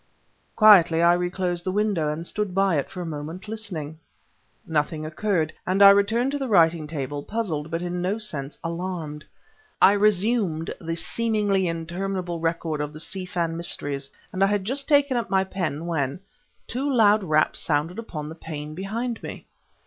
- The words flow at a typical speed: Yes, average, 170 wpm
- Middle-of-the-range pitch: Yes, medium, 175 Hz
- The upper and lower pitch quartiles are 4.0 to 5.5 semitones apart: Yes, average, 4.4 semitones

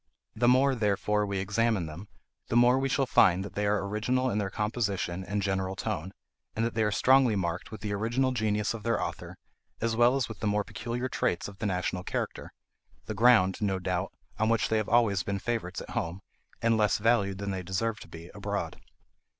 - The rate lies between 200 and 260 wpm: Yes, fast, 205 wpm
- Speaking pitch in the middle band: No, low, 105 Hz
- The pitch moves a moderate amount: Yes, average, 3.1 semitones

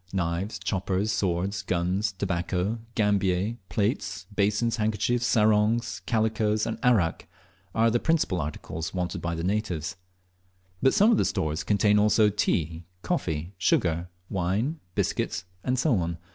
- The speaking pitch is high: No, low, 100 Hz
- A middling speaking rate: No, slow, 125 wpm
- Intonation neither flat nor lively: Yes, average, 3.9 semitones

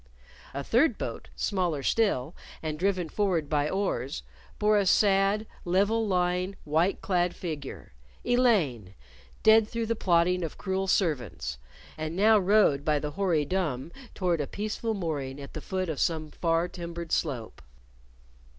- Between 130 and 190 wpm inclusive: Yes, average, 145 wpm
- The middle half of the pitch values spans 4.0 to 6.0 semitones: Yes, average, 4.8 semitones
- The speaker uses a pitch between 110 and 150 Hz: No, medium, 175 Hz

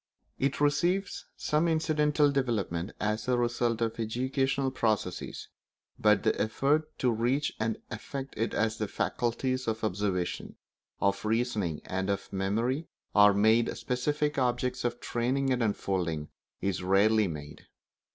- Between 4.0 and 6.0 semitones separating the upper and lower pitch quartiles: Yes, average, 4.5 semitones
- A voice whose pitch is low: Yes, low, 115 Hz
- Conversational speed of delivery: No, slow, 130 wpm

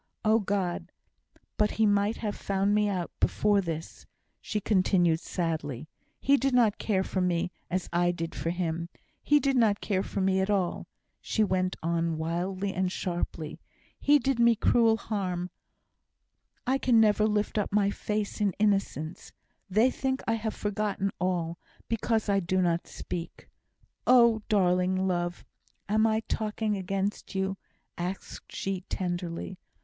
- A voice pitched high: Yes, high, 195 Hz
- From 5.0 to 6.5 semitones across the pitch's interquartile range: No, average, 3.2 semitones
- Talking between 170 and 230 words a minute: No, average, 155 wpm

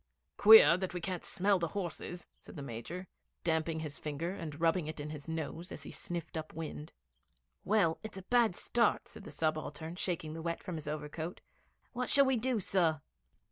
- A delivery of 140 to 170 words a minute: No, average, 190 wpm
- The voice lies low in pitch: No, medium, 165 Hz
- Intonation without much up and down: No, average, 3.3 semitones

